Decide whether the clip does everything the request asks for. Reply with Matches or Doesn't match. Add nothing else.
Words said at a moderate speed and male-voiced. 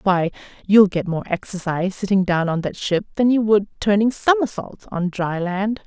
Doesn't match